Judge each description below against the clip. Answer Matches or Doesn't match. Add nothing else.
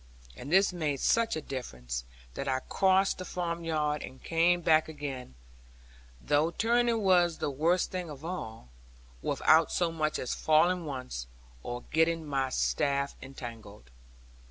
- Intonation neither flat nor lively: Matches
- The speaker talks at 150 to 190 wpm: Doesn't match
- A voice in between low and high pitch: Matches